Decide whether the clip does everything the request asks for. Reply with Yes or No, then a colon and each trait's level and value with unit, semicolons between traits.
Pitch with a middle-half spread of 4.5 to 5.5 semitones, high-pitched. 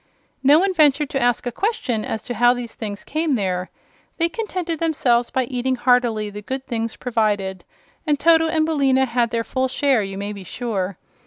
Yes: average, 5.0 semitones; high, 245 Hz